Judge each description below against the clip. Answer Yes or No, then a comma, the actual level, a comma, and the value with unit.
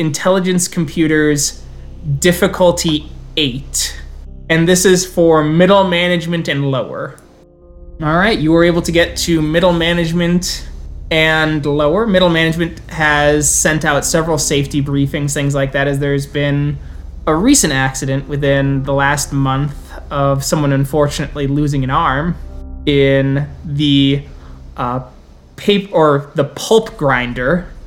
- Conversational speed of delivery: No, slow, 125 wpm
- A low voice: No, medium, 145 Hz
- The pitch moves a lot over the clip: No, average, 3.6 semitones